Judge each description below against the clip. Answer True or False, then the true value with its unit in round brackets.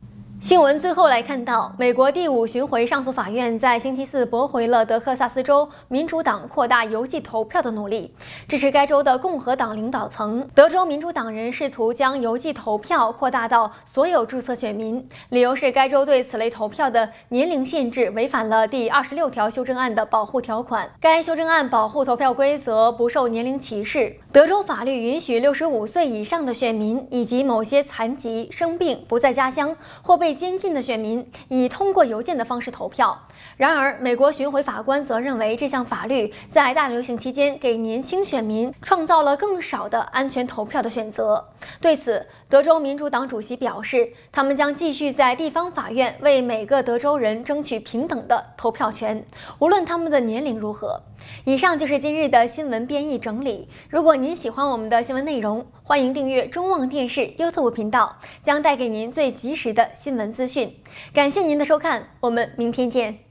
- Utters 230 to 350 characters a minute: True (295 characters per minute)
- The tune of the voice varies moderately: True (3.6 semitones)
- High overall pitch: True (260 Hz)